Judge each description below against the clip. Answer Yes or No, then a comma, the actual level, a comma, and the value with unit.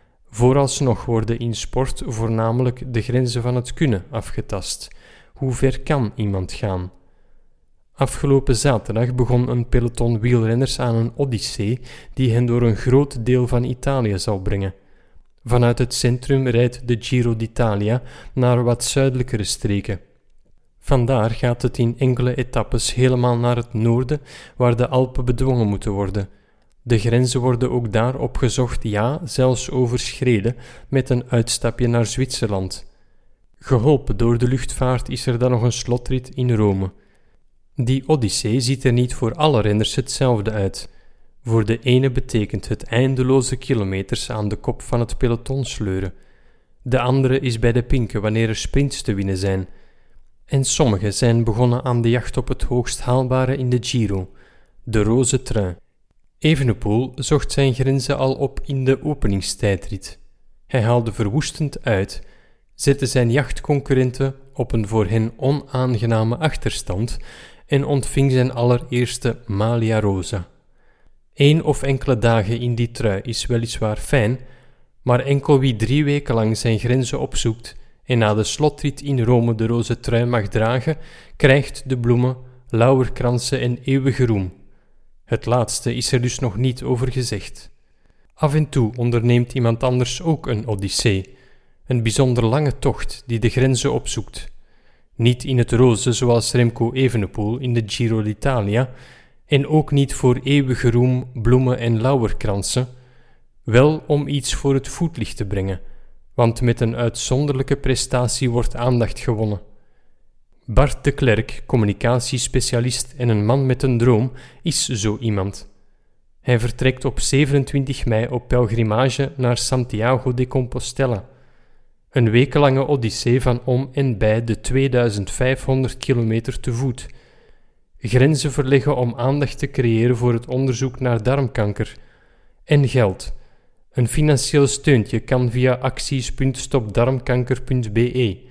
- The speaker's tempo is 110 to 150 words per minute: Yes, average, 140 wpm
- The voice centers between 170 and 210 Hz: No, low, 125 Hz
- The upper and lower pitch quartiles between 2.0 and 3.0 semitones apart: Yes, narrow, 2.4 semitones